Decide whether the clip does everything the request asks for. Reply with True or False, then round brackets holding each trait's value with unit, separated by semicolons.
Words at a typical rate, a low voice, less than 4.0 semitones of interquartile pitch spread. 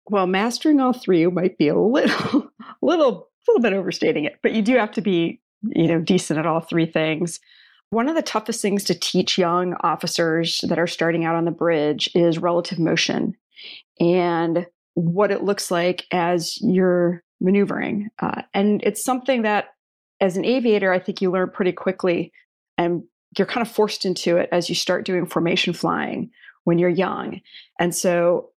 False (180 wpm; 180 Hz; 3.6 semitones)